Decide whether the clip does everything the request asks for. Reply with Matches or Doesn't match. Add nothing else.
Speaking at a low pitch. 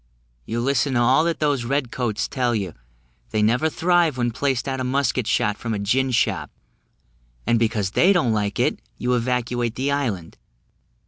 Matches